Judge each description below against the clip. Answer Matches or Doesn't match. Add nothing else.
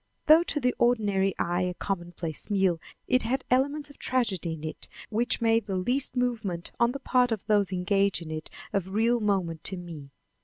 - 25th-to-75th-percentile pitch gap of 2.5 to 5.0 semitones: Doesn't match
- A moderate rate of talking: Matches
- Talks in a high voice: Matches